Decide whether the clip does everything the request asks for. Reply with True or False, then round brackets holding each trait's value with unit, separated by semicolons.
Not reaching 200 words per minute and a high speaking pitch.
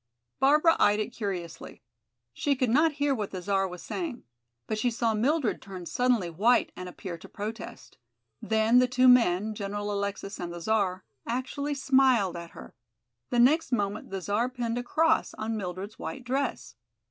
True (170 wpm; 220 Hz)